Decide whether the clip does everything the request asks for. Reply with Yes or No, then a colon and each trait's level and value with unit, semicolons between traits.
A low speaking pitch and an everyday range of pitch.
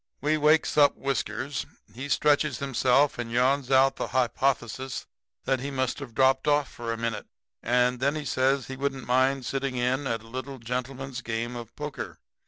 No: low, 130 Hz; narrow, 2.0 semitones